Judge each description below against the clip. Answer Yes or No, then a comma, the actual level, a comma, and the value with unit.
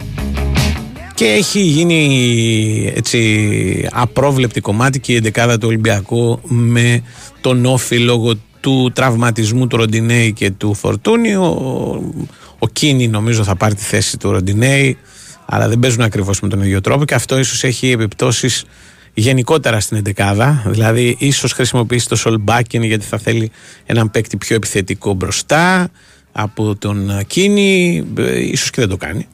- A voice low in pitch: Yes, low, 115 Hz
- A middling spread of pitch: Yes, average, 3.2 semitones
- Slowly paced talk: No, average, 140 wpm